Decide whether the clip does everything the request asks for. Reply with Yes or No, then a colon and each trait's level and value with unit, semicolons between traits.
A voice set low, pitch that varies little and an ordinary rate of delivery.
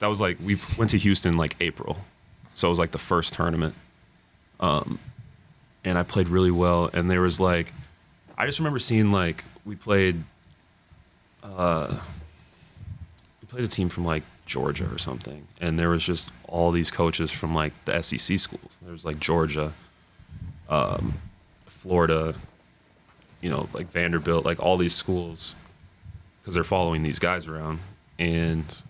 Yes: very low, 85 Hz; narrow, 2.1 semitones; average, 160 wpm